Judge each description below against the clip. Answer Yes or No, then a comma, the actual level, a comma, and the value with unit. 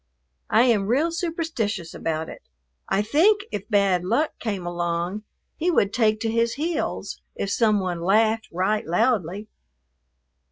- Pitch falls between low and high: No, high, 215 Hz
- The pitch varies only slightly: No, average, 4.9 semitones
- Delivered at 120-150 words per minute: Yes, average, 145 wpm